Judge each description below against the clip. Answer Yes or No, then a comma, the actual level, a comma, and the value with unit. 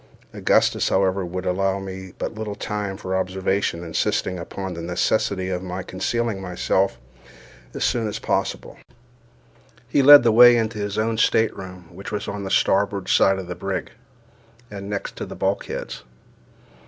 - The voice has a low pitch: Yes, very low, 95 Hz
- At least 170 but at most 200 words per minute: No, average, 155 wpm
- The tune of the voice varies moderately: No, narrow, 2.1 semitones